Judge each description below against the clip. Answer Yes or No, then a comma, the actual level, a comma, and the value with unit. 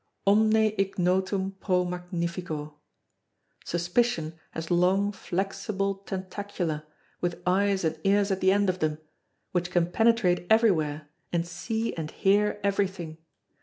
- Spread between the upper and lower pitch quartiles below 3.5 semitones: Yes, narrow, 2.6 semitones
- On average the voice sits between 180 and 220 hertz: Yes, medium, 185 Hz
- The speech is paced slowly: Yes, slow, 120 wpm